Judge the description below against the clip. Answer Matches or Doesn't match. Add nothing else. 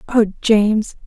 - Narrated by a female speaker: Matches